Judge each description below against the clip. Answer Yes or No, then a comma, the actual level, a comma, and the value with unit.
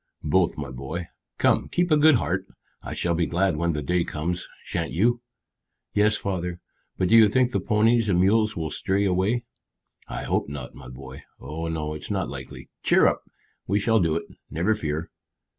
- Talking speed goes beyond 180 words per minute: Yes, average, 190 wpm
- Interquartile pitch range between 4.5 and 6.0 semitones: Yes, average, 5.3 semitones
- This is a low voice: Yes, very low, 90 Hz